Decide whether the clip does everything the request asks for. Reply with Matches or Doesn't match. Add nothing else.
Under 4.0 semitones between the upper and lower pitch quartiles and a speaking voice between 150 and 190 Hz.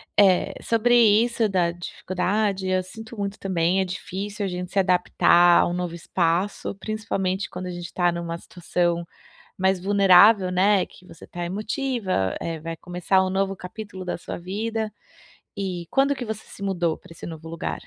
Matches